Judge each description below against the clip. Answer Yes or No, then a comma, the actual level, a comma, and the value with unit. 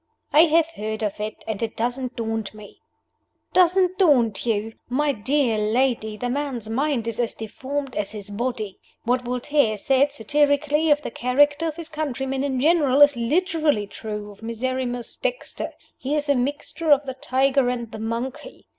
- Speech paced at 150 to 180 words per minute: Yes, average, 170 wpm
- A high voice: Yes, very high, 255 Hz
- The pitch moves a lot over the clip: No, average, 4.5 semitones